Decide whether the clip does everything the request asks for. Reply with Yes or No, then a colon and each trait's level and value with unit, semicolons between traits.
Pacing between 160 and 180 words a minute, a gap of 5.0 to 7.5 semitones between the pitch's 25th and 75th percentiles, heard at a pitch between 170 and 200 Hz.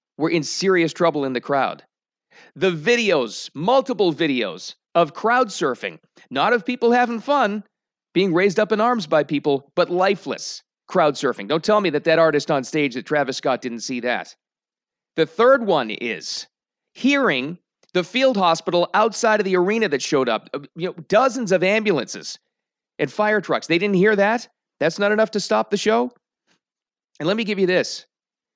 Yes: average, 175 wpm; wide, 5.4 semitones; high, 190 Hz